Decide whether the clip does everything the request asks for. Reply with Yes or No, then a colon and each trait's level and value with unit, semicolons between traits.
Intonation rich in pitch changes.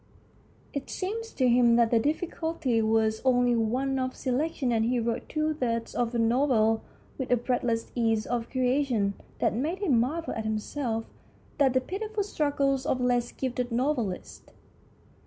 No: average, 3.5 semitones